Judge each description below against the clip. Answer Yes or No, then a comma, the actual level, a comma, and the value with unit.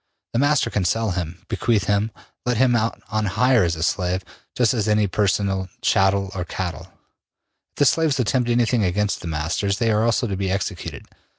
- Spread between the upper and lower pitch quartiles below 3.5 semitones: No, average, 3.8 semitones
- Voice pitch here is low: Yes, low, 105 Hz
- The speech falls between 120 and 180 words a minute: No, average, 195 wpm